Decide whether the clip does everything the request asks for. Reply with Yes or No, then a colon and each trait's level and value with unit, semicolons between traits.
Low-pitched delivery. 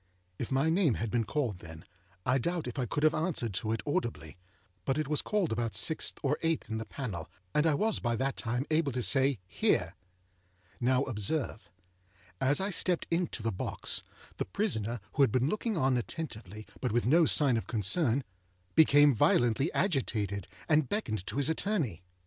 Yes: low, 130 Hz